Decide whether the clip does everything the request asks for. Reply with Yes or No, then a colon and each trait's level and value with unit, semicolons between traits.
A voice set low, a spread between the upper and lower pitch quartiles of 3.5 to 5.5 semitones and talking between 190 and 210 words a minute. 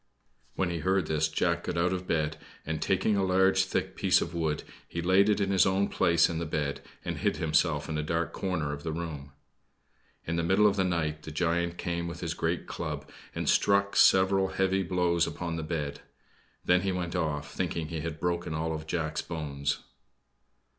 No: very low, 85 Hz; average, 2.9 semitones; average, 200 wpm